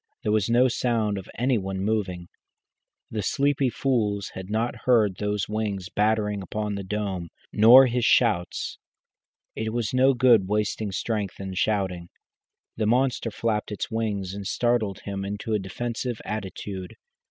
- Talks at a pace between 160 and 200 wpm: No, average, 150 wpm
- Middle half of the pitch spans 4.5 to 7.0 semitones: No, average, 3.1 semitones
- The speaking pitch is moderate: No, low, 105 Hz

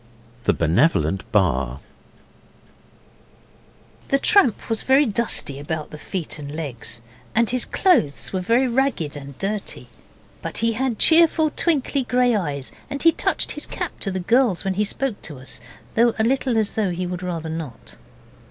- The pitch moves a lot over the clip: Yes, wide, 8.9 semitones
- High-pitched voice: Yes, high, 200 Hz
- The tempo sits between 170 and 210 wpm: No, average, 160 wpm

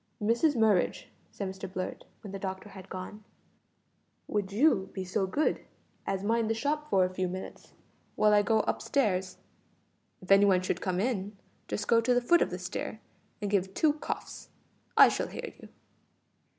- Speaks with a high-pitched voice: Yes, high, 200 Hz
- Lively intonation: No, average, 3.2 semitones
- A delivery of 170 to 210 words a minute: Yes, average, 180 wpm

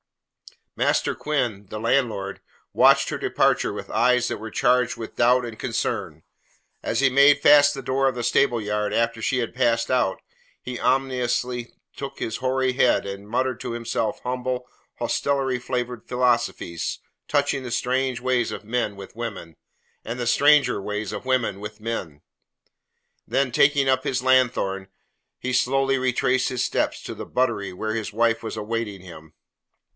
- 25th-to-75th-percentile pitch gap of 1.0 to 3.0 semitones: Yes, average, 2.7 semitones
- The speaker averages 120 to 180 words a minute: Yes, average, 160 wpm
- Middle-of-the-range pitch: No, low, 125 Hz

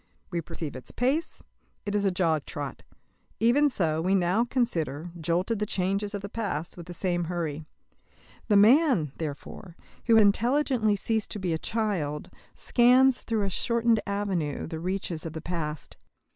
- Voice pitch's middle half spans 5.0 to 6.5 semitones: Yes, wide, 5.4 semitones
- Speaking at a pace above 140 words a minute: Yes, average, 165 wpm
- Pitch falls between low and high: No, high, 195 Hz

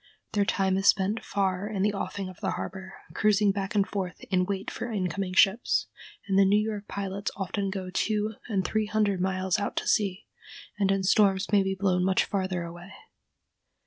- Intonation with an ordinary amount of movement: No, narrow, 1.4 semitones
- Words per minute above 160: Yes, average, 190 wpm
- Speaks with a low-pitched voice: No, high, 195 Hz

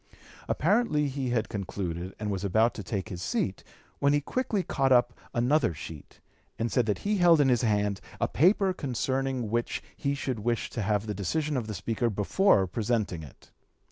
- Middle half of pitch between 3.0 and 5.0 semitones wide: No, wide, 5.4 semitones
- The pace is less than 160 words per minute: No, average, 185 wpm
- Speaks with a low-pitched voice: Yes, low, 120 Hz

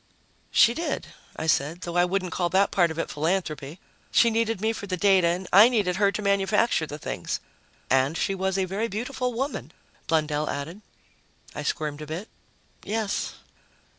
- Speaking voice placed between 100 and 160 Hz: No, high, 190 Hz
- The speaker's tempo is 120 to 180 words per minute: Yes, average, 175 wpm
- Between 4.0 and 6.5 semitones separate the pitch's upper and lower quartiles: Yes, average, 4.6 semitones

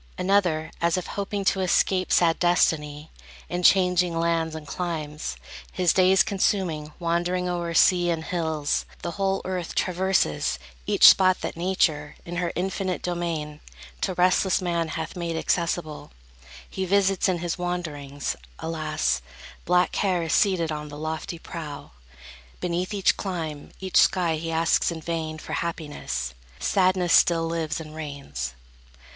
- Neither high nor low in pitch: Yes, medium, 170 Hz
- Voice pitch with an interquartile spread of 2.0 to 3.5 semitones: Yes, narrow, 2.5 semitones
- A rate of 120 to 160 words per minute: Yes, average, 140 wpm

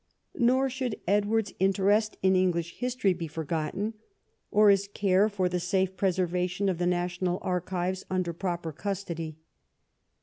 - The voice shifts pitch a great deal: No, narrow, 2.5 semitones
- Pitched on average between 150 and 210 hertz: Yes, medium, 185 Hz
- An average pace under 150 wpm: Yes, slow, 135 wpm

